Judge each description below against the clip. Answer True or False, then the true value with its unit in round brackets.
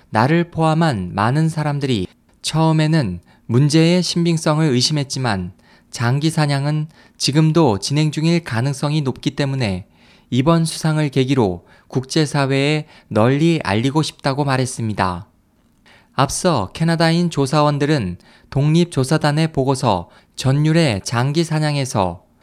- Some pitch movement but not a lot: True (4.7 semitones)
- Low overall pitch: False (145 Hz)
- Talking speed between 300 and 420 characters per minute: False (275 characters per minute)